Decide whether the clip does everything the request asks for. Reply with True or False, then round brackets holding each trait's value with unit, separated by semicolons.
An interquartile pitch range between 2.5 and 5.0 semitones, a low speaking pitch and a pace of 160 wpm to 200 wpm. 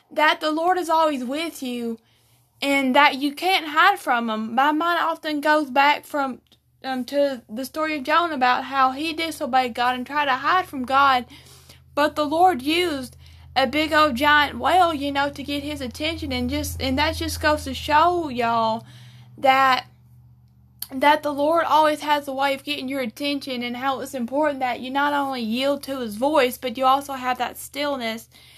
False (3.1 semitones; 280 Hz; 190 wpm)